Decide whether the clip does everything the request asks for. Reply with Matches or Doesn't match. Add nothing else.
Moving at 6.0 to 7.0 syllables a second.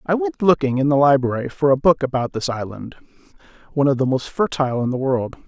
Matches